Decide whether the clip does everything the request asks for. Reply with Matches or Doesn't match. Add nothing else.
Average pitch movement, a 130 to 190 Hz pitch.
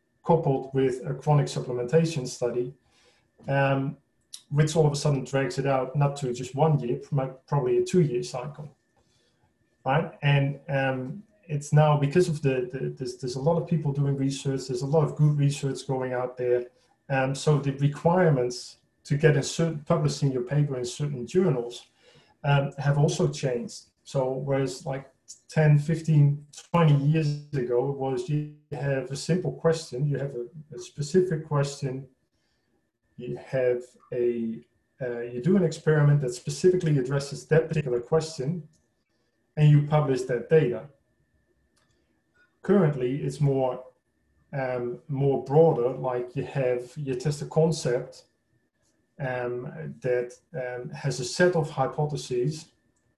Matches